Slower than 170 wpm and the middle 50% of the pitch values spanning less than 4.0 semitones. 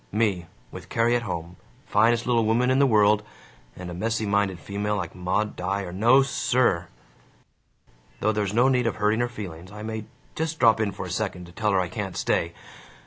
No: average, 195 wpm; average, 3.6 semitones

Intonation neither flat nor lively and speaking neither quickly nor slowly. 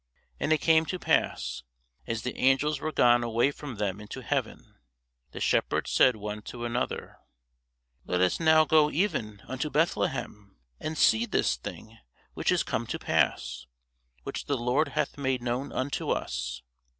No: wide, 6.1 semitones; average, 160 wpm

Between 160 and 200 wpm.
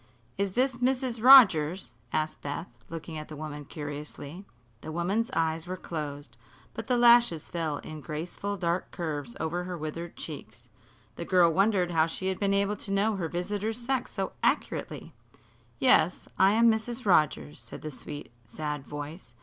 Yes: average, 165 wpm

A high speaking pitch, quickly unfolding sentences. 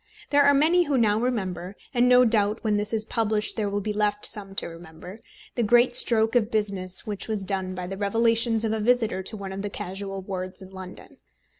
Yes: high, 210 Hz; fast, 215 wpm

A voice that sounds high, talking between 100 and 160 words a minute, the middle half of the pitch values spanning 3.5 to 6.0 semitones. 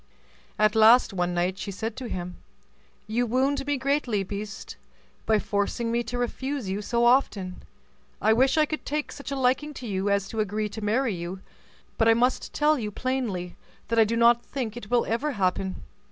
No: high, 225 Hz; average, 195 wpm; average, 4.2 semitones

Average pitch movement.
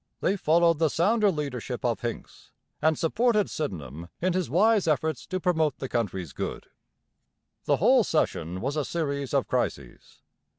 No: wide, 6.5 semitones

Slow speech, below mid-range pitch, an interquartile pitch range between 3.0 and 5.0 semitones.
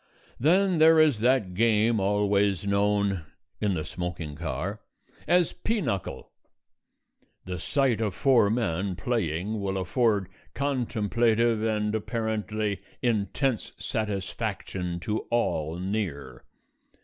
Yes: slow, 105 wpm; low, 105 Hz; average, 3.6 semitones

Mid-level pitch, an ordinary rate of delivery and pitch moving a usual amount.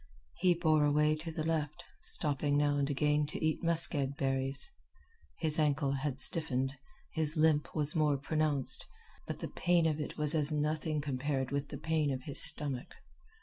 No: medium, 150 Hz; average, 170 wpm; narrow, 1.8 semitones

